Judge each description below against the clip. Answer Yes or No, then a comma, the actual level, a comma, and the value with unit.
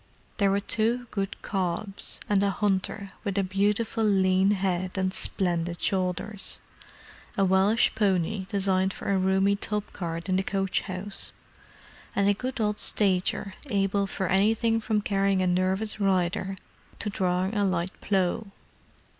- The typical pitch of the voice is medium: No, high, 195 Hz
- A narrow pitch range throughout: Yes, narrow, 1.6 semitones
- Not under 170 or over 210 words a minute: No, average, 145 wpm